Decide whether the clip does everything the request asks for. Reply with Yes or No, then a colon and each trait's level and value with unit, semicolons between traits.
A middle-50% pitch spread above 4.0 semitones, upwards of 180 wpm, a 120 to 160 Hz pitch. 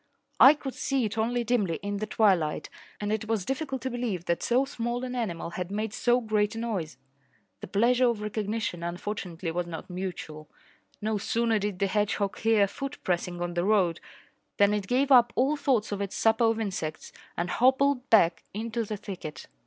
No: average, 4.4 semitones; average, 190 wpm; high, 215 Hz